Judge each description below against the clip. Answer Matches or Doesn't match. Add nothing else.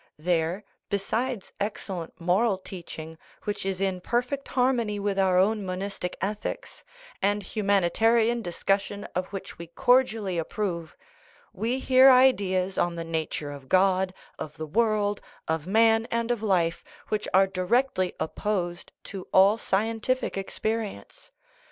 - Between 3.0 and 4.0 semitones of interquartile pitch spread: Matches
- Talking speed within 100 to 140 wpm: Matches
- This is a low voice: Doesn't match